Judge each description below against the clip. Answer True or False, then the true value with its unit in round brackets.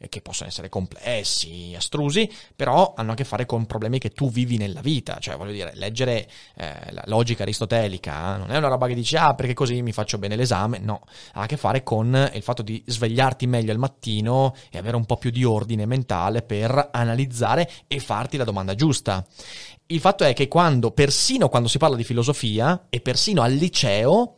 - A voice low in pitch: True (120 Hz)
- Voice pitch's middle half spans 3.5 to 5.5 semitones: True (4.1 semitones)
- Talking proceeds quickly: True (200 wpm)